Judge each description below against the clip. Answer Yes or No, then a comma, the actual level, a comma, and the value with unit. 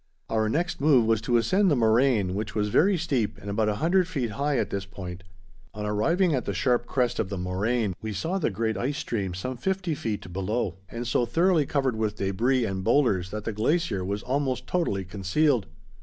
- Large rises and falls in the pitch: Yes, wide, 5.7 semitones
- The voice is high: No, low, 115 Hz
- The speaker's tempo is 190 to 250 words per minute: Yes, fast, 205 wpm